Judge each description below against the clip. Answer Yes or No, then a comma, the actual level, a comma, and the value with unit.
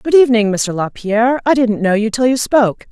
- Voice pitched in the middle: No, high, 230 Hz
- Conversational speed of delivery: No, fast, 245 wpm